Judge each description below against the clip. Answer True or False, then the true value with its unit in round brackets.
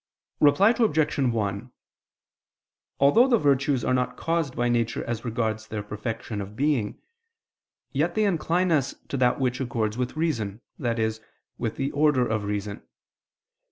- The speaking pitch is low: True (125 Hz)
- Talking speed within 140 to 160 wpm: True (145 wpm)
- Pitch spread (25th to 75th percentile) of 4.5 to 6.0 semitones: True (4.9 semitones)